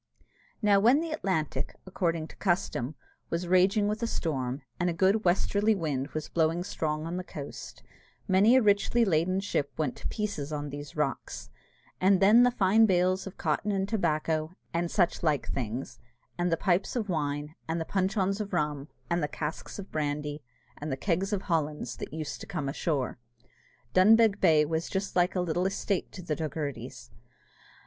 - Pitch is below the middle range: No, medium, 175 Hz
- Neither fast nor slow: Yes, average, 180 wpm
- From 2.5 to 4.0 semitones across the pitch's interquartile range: No, average, 4.4 semitones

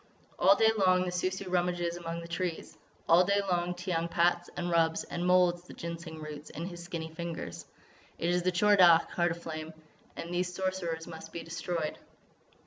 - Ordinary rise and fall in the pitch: No, narrow, 1.5 semitones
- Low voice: No, medium, 175 Hz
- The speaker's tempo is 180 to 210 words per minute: Yes, average, 190 wpm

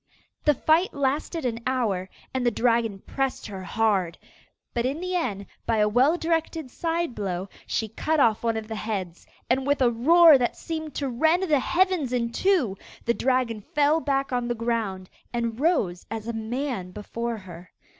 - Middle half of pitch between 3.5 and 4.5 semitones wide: No, average, 5.3 semitones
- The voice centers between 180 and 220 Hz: No, high, 240 Hz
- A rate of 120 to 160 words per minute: No, average, 180 wpm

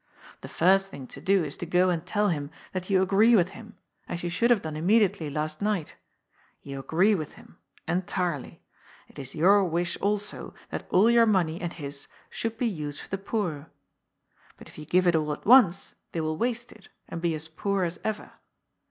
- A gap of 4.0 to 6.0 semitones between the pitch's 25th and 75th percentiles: Yes, average, 4.5 semitones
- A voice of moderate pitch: Yes, medium, 180 Hz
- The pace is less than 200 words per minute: No, fast, 205 wpm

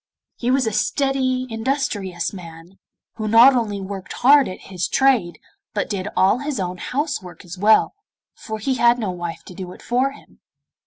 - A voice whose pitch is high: Yes, high, 220 Hz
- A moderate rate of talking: Yes, average, 180 wpm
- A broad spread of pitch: Yes, wide, 5.8 semitones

